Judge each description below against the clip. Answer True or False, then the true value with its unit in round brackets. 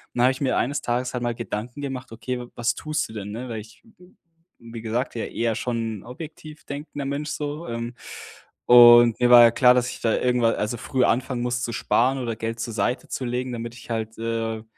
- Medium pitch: False (120 Hz)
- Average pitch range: False (1.9 semitones)